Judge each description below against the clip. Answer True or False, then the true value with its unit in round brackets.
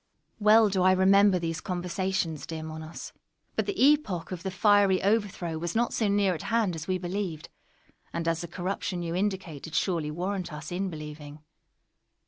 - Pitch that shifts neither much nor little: True (3.3 semitones)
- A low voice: False (180 Hz)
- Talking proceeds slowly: False (180 wpm)